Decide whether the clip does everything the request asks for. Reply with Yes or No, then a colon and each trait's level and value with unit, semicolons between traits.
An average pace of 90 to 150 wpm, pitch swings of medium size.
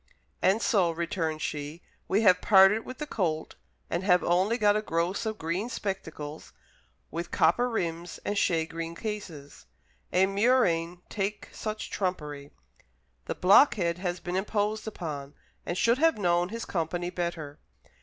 Yes: average, 145 wpm; average, 4.1 semitones